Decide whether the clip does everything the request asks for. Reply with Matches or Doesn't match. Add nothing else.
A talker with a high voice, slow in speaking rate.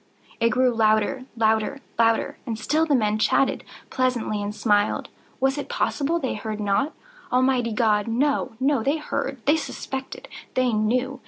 Matches